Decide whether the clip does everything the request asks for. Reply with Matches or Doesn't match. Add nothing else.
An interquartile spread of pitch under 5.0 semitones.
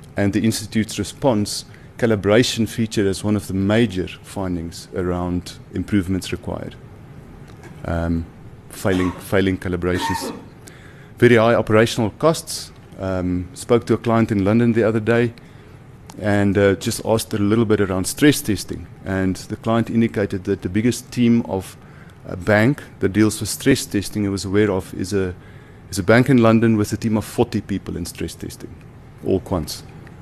Matches